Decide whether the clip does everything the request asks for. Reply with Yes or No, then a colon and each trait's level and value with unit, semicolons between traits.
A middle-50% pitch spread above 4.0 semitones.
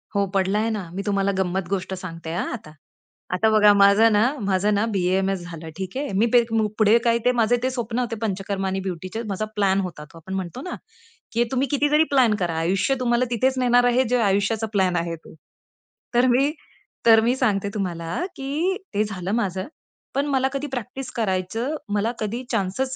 Yes: average, 4.4 semitones